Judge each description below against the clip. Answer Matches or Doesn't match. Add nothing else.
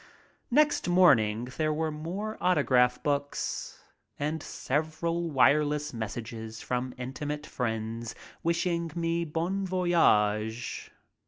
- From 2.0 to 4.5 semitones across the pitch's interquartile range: Doesn't match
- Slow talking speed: Matches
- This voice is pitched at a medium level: Matches